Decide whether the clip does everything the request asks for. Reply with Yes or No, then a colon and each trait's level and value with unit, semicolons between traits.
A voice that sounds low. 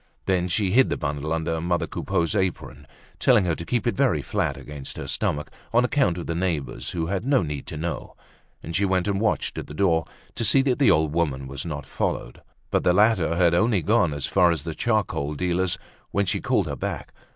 Yes: very low, 85 Hz